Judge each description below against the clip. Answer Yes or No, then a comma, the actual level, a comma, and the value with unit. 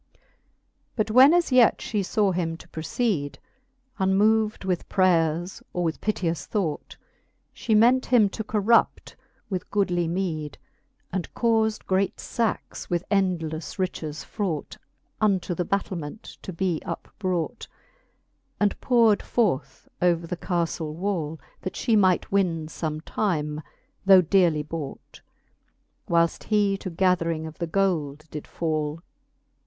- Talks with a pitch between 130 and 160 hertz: No, medium, 185 Hz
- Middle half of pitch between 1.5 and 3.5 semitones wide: No, average, 4.0 semitones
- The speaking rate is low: Yes, slow, 130 wpm